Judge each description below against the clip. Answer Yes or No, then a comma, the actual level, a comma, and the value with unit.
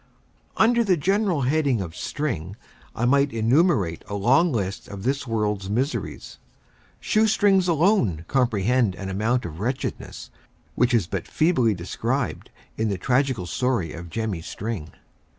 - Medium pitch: No, low, 120 Hz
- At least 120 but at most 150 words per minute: Yes, average, 140 wpm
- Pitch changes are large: Yes, wide, 6.7 semitones